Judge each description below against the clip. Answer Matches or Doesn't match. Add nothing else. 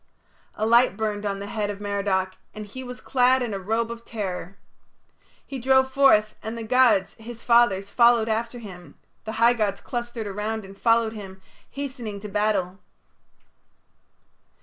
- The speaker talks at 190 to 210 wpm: Doesn't match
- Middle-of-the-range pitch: Doesn't match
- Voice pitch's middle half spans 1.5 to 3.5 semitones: Matches